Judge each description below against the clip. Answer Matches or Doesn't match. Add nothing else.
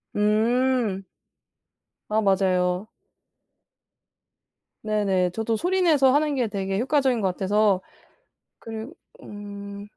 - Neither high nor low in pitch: Doesn't match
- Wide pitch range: Doesn't match